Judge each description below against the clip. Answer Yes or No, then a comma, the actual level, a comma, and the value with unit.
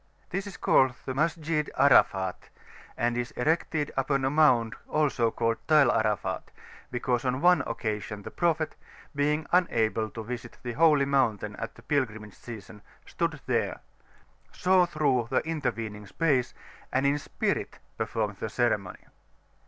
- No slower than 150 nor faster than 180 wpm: No, average, 140 wpm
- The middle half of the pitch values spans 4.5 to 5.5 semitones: Yes, average, 5.2 semitones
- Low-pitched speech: Yes, low, 130 Hz